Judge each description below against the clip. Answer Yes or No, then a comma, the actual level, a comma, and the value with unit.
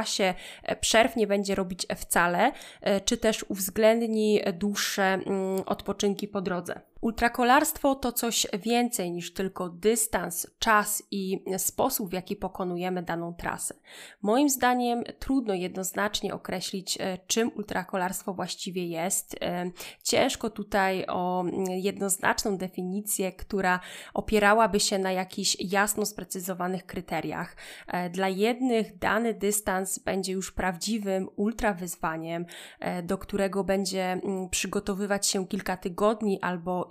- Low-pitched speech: No, high, 195 Hz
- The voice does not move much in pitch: Yes, narrow, 2.3 semitones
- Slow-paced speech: Yes, slow, 105 wpm